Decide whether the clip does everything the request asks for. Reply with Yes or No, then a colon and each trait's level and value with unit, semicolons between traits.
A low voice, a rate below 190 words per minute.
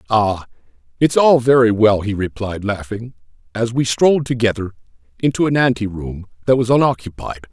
Yes: low, 115 Hz; average, 150 wpm